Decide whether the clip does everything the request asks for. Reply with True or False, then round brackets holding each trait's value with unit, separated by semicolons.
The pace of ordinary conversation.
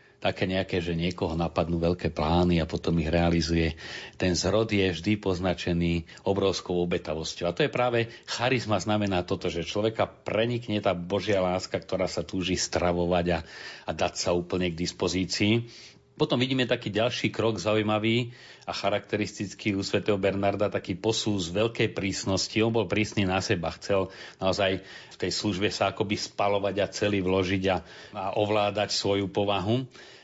True (155 wpm)